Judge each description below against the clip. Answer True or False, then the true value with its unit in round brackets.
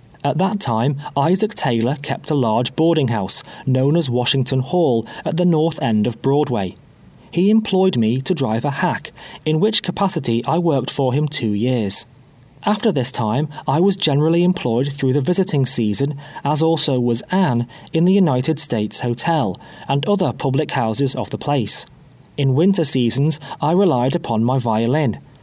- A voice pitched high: False (140 Hz)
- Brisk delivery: False (170 wpm)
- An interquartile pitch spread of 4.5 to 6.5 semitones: True (4.9 semitones)